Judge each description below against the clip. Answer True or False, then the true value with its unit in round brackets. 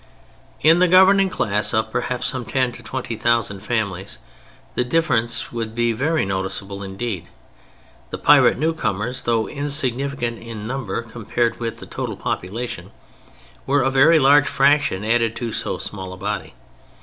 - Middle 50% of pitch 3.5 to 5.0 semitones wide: True (4.1 semitones)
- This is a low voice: True (120 Hz)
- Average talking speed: True (150 wpm)